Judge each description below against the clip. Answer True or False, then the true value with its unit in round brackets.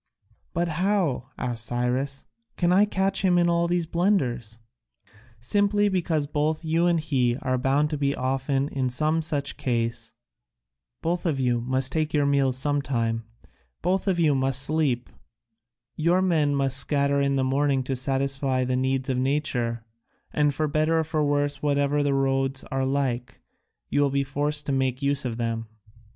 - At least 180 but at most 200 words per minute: False (165 wpm)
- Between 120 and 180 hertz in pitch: True (140 Hz)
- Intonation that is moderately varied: True (3.1 semitones)